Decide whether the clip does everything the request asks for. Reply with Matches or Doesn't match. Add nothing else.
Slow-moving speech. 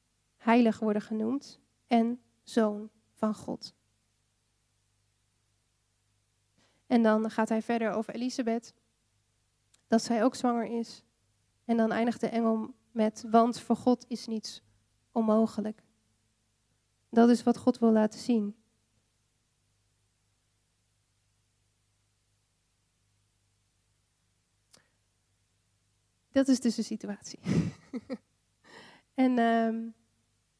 Matches